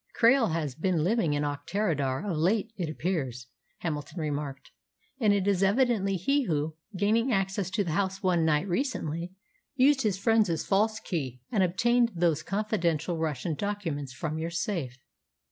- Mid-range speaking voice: Yes, medium, 180 Hz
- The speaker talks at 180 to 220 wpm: No, average, 155 wpm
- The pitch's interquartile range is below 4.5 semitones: No, average, 5.1 semitones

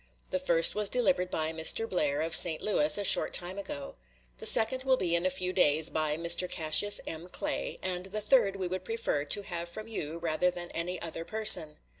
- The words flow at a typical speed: No, fast, 210 wpm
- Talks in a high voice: No, medium, 180 Hz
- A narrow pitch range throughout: No, average, 3.8 semitones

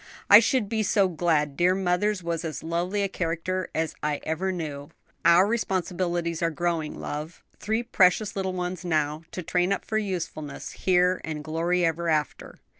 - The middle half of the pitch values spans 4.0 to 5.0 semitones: No, narrow, 2.6 semitones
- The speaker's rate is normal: Yes, average, 165 wpm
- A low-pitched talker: No, medium, 175 Hz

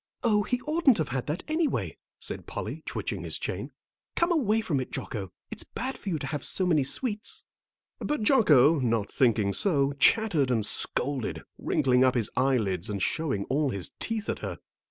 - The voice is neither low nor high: Yes, medium, 145 Hz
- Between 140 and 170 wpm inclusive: No, average, 180 wpm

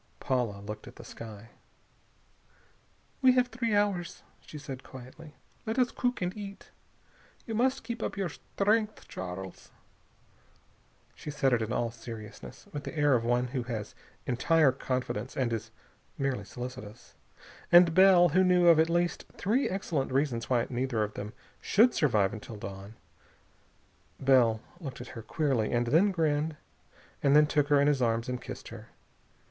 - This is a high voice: No, low, 135 Hz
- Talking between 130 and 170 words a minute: Yes, average, 160 wpm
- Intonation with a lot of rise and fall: Yes, wide, 7.1 semitones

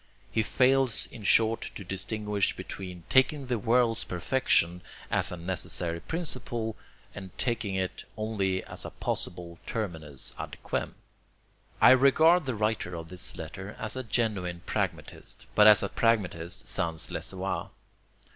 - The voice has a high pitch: No, low, 105 Hz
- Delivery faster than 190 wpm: No, average, 140 wpm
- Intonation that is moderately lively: Yes, average, 4.9 semitones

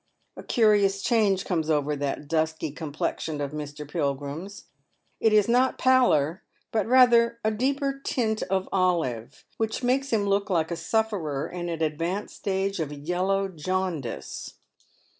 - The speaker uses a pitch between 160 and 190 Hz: Yes, medium, 185 Hz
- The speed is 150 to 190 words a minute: No, average, 140 wpm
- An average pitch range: No, wide, 6.0 semitones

